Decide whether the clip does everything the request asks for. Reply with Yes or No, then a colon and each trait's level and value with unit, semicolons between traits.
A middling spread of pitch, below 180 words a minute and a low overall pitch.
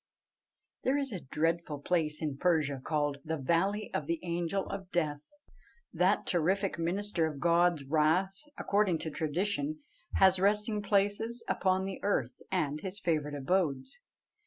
No: average, 4.4 semitones; average, 140 wpm; medium, 175 Hz